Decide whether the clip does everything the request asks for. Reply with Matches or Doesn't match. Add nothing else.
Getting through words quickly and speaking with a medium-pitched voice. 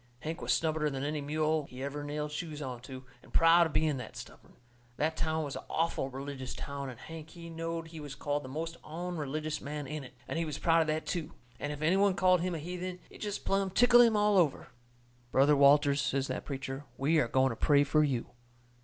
Matches